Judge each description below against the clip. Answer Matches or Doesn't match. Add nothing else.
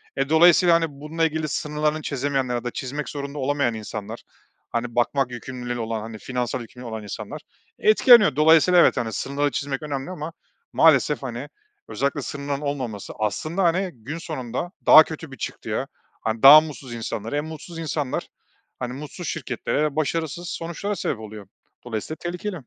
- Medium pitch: Matches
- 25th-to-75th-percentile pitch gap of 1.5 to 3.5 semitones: Doesn't match